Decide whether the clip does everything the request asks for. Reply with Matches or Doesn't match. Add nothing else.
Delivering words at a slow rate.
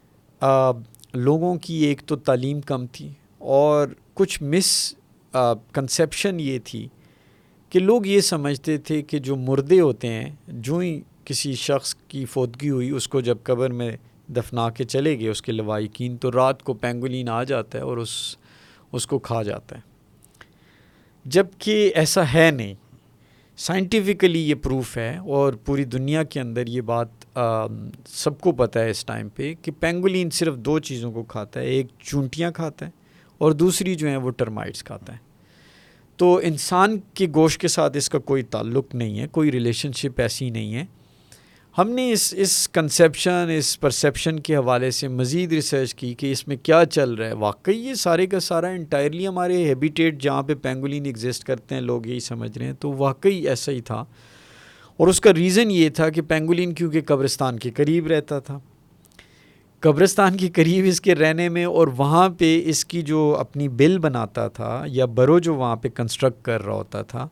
Doesn't match